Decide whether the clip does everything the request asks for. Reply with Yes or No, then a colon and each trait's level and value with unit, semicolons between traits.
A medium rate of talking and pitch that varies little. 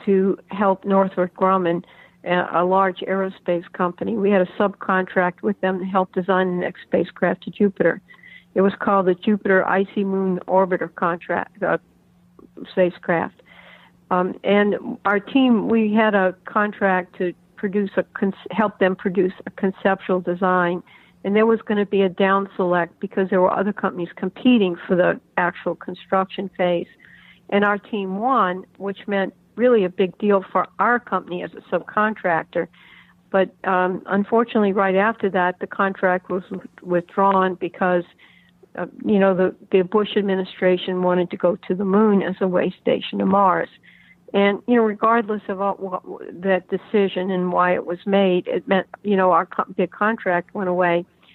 Yes: average, 165 wpm; narrow, 1.8 semitones